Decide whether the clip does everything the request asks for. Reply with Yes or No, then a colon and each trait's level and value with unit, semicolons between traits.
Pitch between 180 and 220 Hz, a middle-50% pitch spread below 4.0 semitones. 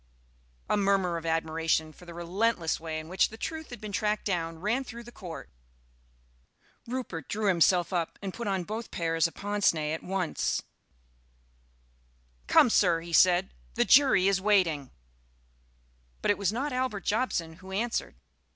No: high, 190 Hz; average, 4.3 semitones